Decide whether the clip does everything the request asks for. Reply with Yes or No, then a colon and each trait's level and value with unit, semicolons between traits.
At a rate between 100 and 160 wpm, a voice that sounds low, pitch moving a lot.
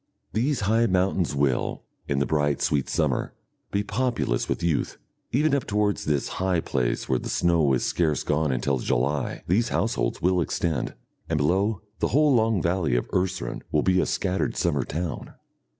No: average, 170 wpm; very low, 85 Hz; wide, 5.9 semitones